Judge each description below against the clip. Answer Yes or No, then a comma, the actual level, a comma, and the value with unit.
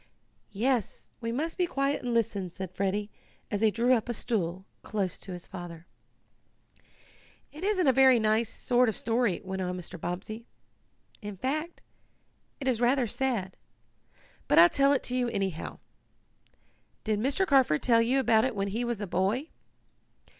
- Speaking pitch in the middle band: No, high, 225 Hz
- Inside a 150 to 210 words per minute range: Yes, average, 160 wpm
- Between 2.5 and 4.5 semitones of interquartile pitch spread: No, average, 5.2 semitones